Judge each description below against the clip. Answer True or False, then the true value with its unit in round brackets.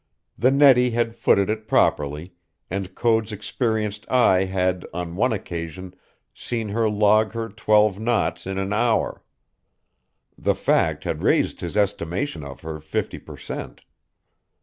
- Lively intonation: False (3.6 semitones)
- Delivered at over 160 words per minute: False (140 wpm)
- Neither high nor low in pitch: False (105 Hz)